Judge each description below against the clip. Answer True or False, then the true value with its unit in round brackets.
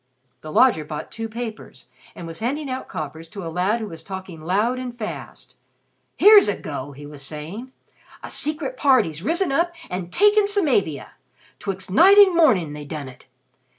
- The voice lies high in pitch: True (205 Hz)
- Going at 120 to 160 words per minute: False (175 wpm)